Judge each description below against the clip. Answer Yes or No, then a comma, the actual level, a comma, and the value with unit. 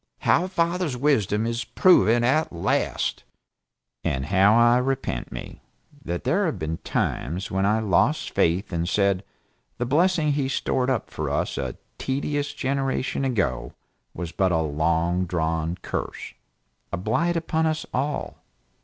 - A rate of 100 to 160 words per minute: Yes, average, 145 wpm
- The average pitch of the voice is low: Yes, low, 115 Hz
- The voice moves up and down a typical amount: No, wide, 8.6 semitones